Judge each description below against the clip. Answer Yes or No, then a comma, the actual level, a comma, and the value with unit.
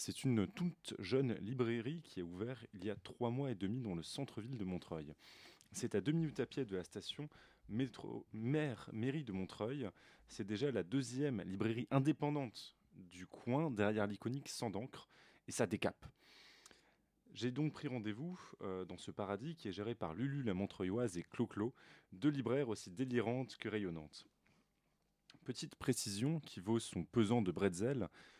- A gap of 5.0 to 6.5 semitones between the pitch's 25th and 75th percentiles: Yes, wide, 5.5 semitones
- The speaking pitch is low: Yes, low, 120 Hz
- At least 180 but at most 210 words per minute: No, average, 165 wpm